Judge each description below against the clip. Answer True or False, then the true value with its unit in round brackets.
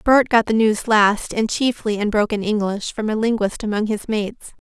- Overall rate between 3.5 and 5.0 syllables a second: True (4.9 syllables/s)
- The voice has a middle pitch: False (215 Hz)